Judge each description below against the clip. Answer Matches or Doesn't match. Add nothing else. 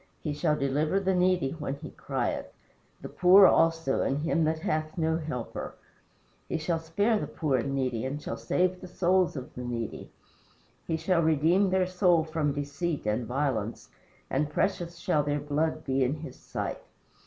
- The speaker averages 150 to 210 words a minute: Matches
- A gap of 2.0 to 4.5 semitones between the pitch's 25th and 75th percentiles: Matches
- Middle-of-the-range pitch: Matches